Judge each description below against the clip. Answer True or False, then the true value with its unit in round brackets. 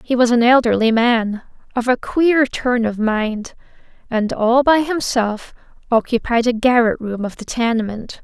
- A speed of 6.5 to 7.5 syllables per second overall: False (4.3 syllables/s)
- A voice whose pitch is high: True (235 Hz)